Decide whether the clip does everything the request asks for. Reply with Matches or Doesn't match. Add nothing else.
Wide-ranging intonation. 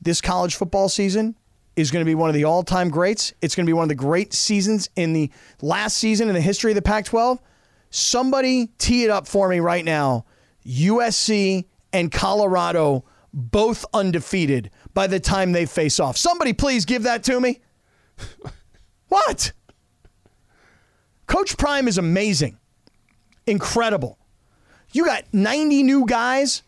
Matches